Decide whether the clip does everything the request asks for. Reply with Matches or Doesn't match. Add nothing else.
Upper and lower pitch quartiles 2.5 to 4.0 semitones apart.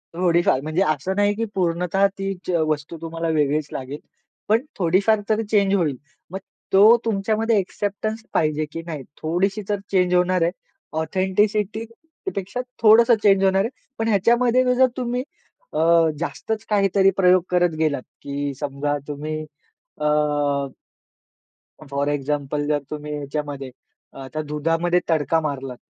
Doesn't match